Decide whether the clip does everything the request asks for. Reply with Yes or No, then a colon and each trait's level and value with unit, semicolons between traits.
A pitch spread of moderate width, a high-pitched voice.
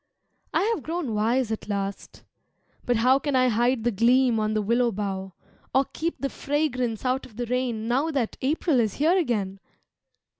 Yes: average, 3.7 semitones; high, 245 Hz